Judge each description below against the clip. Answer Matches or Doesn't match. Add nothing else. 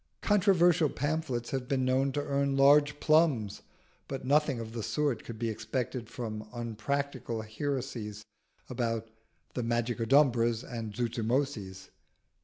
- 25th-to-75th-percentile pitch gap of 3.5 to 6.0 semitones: Matches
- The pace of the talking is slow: Matches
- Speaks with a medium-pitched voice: Doesn't match